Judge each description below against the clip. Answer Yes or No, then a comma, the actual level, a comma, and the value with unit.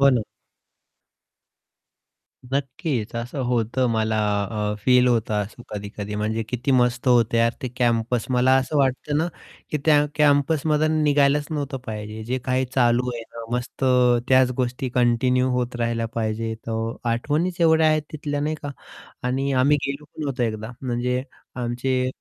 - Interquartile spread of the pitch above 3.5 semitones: No, average, 3.2 semitones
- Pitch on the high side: No, low, 125 Hz